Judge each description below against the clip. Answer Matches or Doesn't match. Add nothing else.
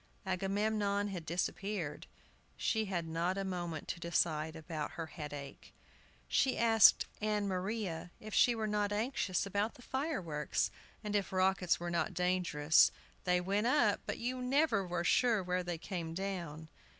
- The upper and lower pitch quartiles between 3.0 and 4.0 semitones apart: Matches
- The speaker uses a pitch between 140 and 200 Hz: Matches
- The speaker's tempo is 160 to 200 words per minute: Doesn't match